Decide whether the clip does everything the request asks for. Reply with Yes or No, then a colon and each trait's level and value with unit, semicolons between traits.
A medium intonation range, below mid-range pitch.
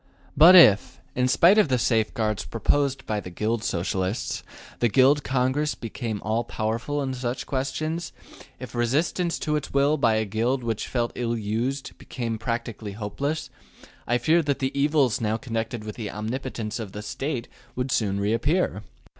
Yes: average, 4.2 semitones; low, 120 Hz